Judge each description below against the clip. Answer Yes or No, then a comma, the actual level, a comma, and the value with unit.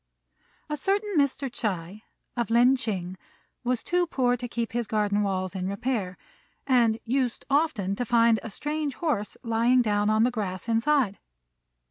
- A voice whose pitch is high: Yes, high, 235 Hz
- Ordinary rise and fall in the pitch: Yes, average, 4.1 semitones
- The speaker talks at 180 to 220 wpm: No, average, 155 wpm